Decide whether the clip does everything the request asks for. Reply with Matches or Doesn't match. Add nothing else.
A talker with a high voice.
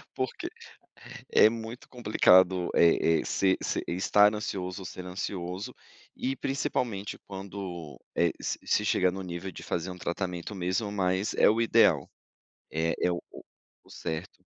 Doesn't match